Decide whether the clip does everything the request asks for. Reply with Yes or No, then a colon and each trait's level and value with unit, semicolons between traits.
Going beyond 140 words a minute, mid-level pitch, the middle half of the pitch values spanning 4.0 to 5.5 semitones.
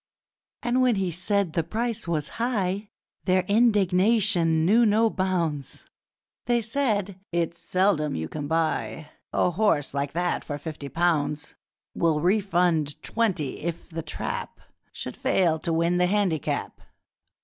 No: slow, 135 wpm; medium, 180 Hz; average, 4.4 semitones